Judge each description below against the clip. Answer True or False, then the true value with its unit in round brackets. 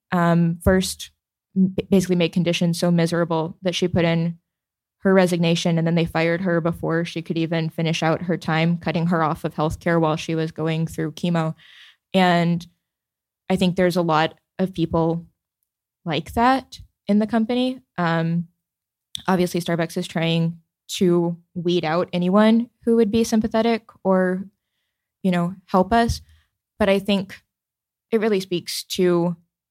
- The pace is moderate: True (150 wpm)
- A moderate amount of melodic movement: False (2.2 semitones)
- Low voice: False (175 Hz)